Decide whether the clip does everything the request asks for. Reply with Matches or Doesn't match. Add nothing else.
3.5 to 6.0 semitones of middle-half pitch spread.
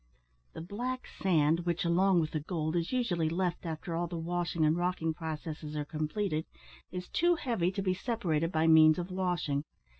Doesn't match